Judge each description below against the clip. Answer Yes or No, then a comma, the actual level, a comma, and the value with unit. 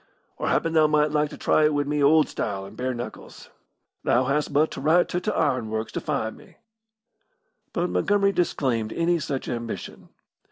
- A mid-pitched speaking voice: Yes, medium, 150 Hz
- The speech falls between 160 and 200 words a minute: Yes, average, 185 wpm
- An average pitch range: Yes, average, 4.6 semitones